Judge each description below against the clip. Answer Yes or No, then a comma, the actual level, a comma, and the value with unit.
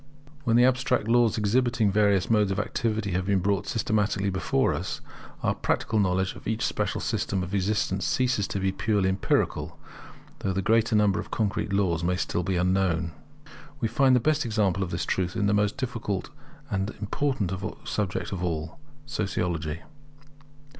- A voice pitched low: Yes, low, 100 Hz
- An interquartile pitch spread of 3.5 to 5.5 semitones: No, average, 3.0 semitones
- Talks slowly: No, average, 170 wpm